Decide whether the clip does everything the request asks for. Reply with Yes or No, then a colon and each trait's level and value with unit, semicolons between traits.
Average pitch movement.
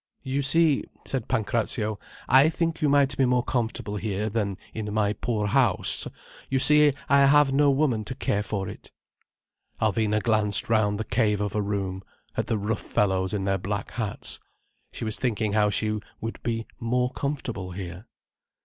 Yes: average, 4.2 semitones